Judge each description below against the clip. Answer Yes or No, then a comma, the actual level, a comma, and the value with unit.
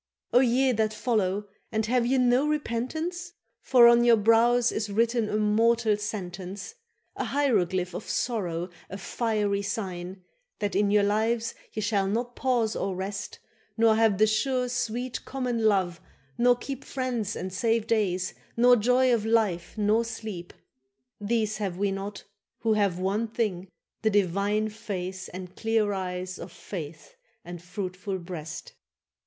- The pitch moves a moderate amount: Yes, average, 3.5 semitones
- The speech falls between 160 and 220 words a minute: No, average, 150 wpm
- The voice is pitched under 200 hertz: No, high, 215 Hz